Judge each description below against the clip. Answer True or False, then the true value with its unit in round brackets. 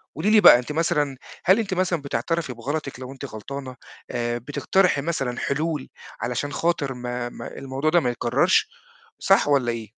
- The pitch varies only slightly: False (4.9 semitones)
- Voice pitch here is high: False (140 Hz)